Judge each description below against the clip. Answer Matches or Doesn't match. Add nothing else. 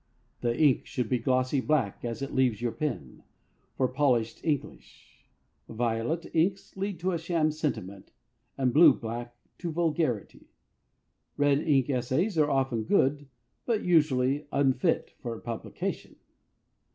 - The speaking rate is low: Matches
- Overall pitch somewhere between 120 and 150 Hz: Matches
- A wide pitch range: Doesn't match